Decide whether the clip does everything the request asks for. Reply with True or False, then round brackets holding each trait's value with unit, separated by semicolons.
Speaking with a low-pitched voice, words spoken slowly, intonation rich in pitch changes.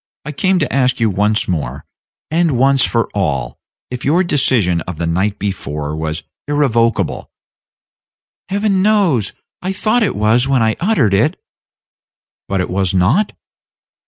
False (115 Hz; 150 wpm; 8.7 semitones)